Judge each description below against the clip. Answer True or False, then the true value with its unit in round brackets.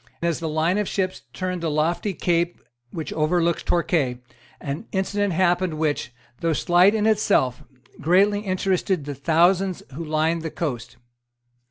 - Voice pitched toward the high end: False (170 Hz)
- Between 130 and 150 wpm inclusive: True (145 wpm)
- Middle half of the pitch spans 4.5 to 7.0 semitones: False (3.2 semitones)